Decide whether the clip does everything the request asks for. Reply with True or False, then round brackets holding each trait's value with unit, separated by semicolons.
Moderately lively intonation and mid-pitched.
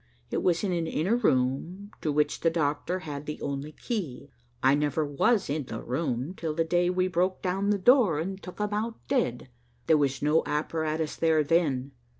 True (4.2 semitones; 160 Hz)